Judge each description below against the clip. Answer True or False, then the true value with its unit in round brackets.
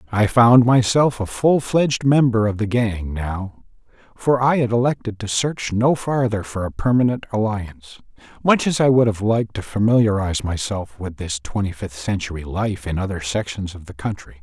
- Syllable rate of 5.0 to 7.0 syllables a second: True (5.1 syllables/s)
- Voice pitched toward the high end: False (110 Hz)